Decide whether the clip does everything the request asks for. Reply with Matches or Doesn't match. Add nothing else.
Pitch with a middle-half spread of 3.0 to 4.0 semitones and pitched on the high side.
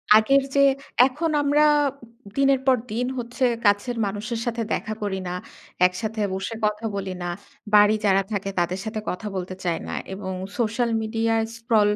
Matches